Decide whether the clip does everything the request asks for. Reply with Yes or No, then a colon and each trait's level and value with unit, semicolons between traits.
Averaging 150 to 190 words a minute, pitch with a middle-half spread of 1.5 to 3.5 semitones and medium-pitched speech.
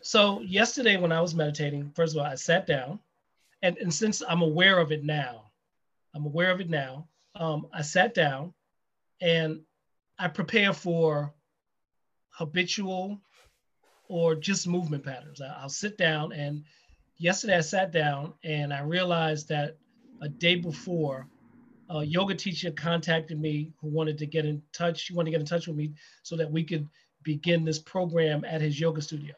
Yes: average, 170 wpm; average, 2.9 semitones; medium, 165 Hz